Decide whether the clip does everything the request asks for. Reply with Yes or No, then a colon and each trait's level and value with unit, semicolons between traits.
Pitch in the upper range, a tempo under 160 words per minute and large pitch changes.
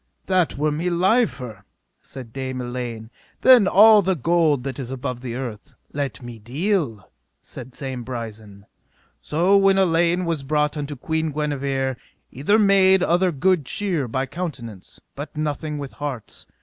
No: medium, 145 Hz; average, 150 wpm; wide, 5.8 semitones